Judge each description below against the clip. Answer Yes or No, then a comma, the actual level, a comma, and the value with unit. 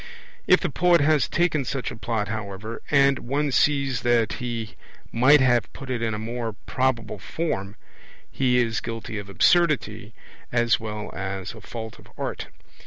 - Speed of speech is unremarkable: Yes, average, 165 wpm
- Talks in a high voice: No, low, 120 Hz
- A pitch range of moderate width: Yes, average, 3.7 semitones